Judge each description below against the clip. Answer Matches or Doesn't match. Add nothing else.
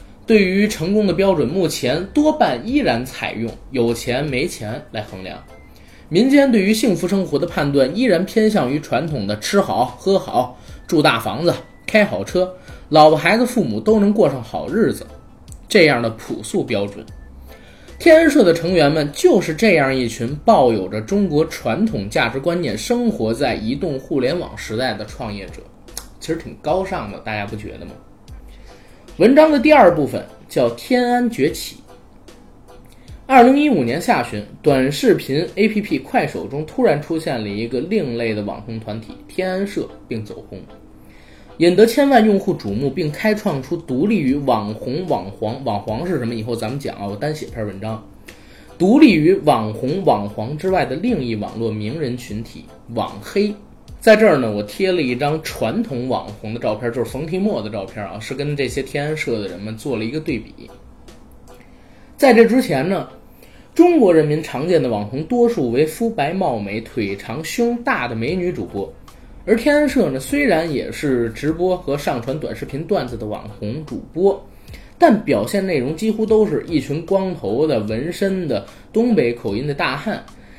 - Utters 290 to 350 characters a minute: Doesn't match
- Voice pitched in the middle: Matches